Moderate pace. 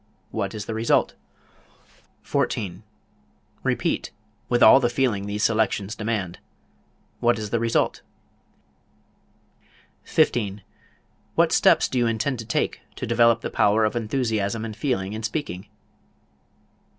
No: slow, 125 wpm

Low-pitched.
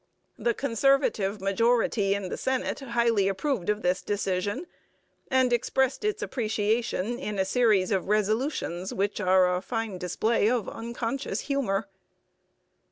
No: high, 220 Hz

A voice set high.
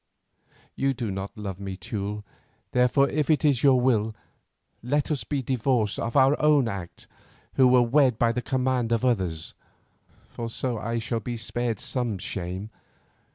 No: low, 120 Hz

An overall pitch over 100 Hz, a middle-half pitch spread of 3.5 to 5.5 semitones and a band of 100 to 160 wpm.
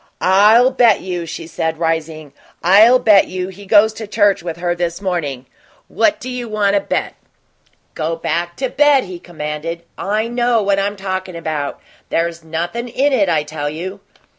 No: medium, 185 Hz; average, 4.5 semitones; average, 170 wpm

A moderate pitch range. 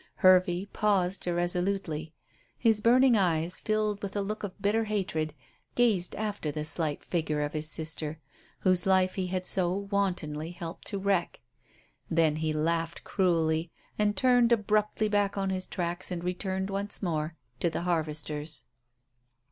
Yes: average, 3.8 semitones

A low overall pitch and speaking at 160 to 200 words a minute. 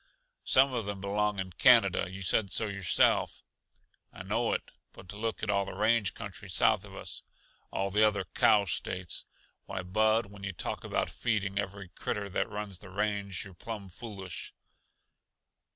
Yes: low, 100 Hz; average, 165 wpm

